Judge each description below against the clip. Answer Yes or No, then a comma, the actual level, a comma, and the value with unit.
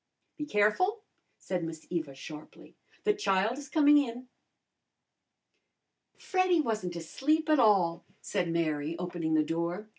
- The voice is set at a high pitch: Yes, high, 195 Hz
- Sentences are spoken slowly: Yes, slow, 125 wpm